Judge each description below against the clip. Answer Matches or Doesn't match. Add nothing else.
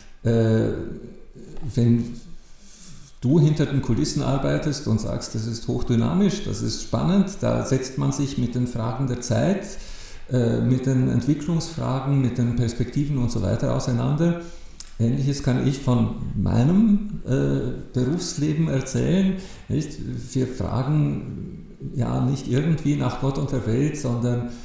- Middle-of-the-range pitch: Doesn't match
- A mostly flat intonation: Doesn't match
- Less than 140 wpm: Matches